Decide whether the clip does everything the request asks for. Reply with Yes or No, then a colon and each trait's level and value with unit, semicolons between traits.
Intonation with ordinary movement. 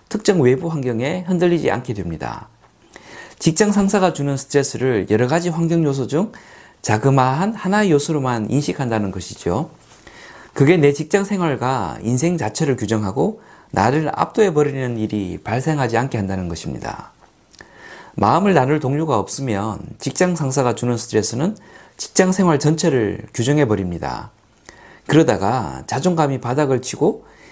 No: wide, 6.2 semitones